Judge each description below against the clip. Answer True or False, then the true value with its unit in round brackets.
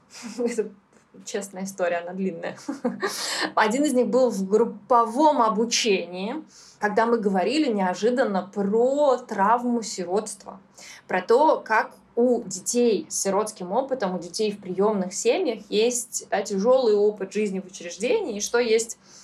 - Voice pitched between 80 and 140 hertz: False (220 Hz)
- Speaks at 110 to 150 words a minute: True (130 wpm)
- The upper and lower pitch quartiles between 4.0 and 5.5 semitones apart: False (3.6 semitones)